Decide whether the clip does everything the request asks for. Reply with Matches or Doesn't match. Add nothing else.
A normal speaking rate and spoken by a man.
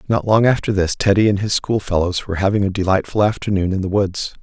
Doesn't match